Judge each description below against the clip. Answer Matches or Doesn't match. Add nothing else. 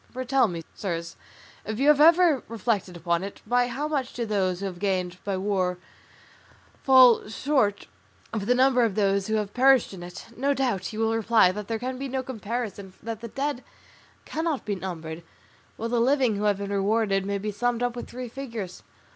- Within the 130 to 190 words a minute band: Doesn't match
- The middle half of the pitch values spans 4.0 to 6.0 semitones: Matches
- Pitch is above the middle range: Matches